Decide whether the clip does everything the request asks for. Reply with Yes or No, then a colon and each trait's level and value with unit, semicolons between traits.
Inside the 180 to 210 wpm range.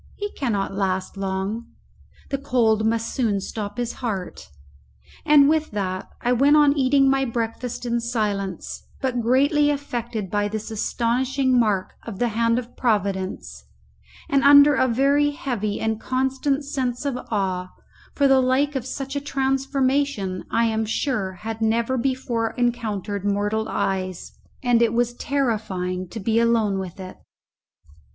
No: average, 145 wpm